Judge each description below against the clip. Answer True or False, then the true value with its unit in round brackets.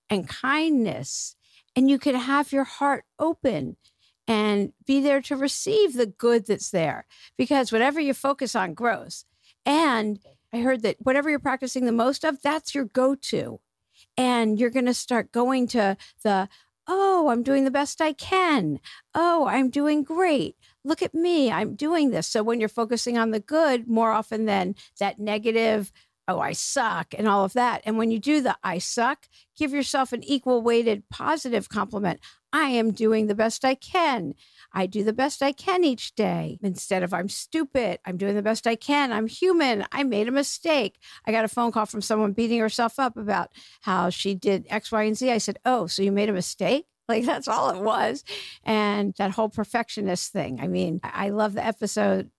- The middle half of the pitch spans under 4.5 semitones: False (4.8 semitones)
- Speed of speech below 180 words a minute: False (195 wpm)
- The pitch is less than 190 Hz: False (235 Hz)